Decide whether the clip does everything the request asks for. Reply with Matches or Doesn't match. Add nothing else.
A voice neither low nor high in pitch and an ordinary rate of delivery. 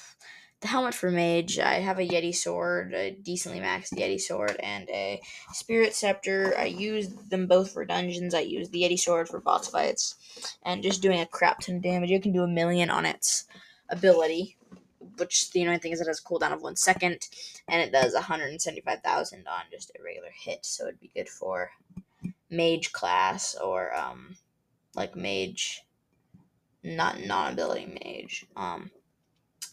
Matches